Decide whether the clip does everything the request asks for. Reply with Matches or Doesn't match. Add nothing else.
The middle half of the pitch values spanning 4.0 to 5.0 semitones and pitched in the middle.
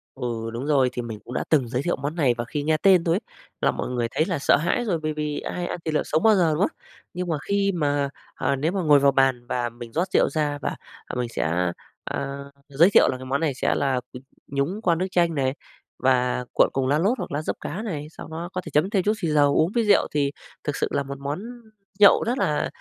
Matches